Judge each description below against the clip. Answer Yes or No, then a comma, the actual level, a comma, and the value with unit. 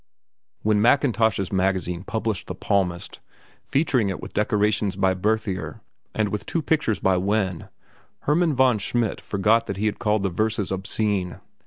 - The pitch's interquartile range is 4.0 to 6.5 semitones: No, narrow, 2.6 semitones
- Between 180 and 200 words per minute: No, average, 150 wpm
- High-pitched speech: No, low, 105 Hz